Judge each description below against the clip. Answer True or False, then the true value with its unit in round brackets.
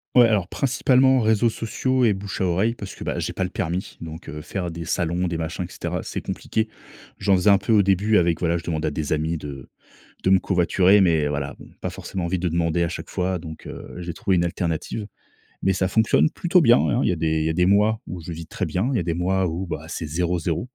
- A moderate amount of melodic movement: True (3.5 semitones)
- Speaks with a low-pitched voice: True (90 Hz)